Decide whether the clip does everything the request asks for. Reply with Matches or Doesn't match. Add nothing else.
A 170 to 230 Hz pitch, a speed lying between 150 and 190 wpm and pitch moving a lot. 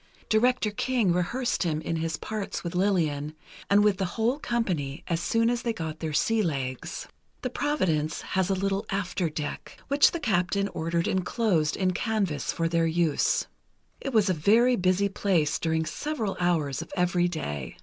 Doesn't match